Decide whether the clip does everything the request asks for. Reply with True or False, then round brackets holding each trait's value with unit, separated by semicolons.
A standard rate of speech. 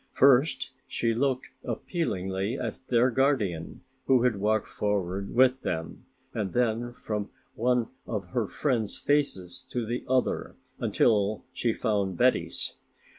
False (125 wpm)